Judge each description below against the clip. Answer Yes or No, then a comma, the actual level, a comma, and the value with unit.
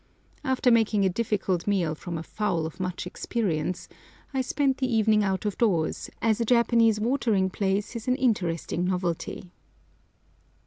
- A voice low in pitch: No, high, 205 Hz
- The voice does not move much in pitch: No, average, 4.3 semitones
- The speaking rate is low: No, average, 150 wpm